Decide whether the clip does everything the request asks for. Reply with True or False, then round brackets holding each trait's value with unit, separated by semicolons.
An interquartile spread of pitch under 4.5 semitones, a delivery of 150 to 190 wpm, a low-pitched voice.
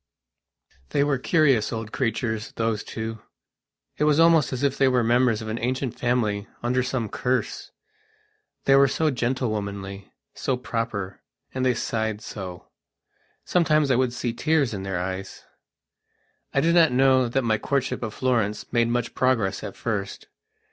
True (3.3 semitones; 155 wpm; 120 Hz)